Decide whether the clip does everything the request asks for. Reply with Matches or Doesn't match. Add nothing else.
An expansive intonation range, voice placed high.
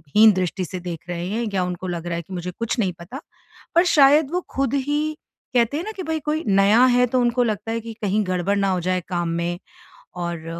Matches